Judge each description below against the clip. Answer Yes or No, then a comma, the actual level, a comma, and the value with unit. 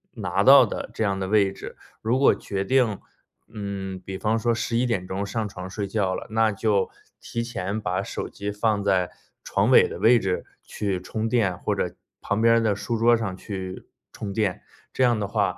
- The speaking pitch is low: Yes, low, 105 Hz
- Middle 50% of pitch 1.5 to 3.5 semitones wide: Yes, average, 2.7 semitones